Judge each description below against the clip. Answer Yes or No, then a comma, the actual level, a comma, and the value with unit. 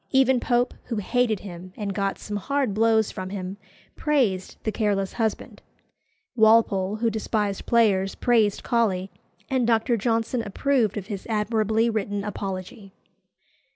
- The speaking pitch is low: No, high, 215 Hz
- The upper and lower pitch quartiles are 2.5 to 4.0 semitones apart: Yes, average, 2.9 semitones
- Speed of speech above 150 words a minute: No, slow, 135 wpm